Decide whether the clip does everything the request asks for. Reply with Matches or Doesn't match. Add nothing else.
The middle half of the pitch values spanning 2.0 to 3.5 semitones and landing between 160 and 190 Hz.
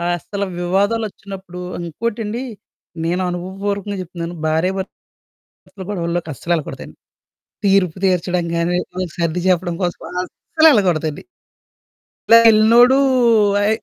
Matches